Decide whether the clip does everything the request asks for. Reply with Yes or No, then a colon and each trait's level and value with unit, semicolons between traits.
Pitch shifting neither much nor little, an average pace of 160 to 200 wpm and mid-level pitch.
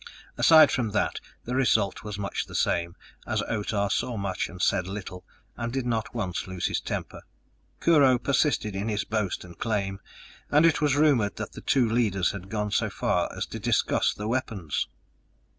No: average, 4.2 semitones; average, 180 wpm; low, 105 Hz